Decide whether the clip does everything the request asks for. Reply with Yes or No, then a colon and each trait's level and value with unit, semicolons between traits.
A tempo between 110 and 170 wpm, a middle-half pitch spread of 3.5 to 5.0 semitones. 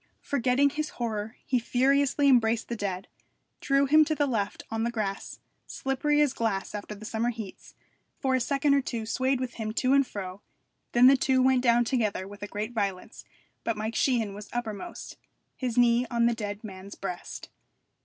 No: average, 185 wpm; average, 3.8 semitones